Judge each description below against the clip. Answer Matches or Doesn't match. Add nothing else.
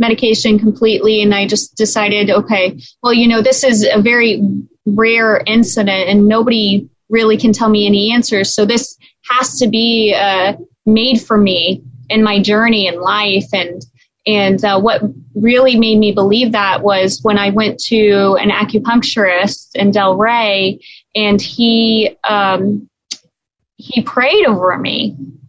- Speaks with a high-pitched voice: Matches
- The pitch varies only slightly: Matches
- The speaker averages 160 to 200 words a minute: Doesn't match